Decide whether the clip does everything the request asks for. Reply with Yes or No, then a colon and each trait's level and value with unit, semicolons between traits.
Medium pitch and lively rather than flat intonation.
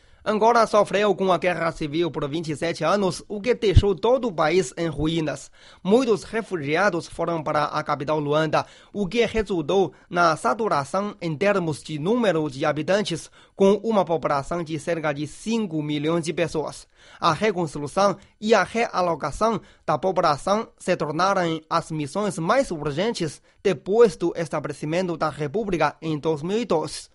No: medium, 170 Hz; average, 4.5 semitones